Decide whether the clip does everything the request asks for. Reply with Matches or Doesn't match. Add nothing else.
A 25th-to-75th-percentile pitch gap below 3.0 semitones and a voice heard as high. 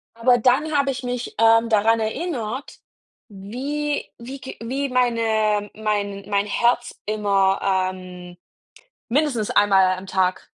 Doesn't match